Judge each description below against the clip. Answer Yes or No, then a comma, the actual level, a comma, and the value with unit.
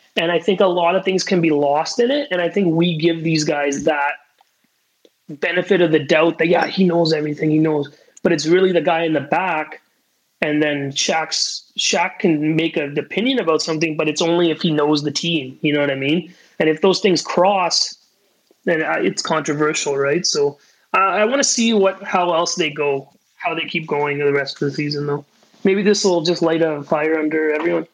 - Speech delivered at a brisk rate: Yes, fast, 215 wpm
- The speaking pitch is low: No, medium, 165 Hz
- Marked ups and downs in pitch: No, average, 2.8 semitones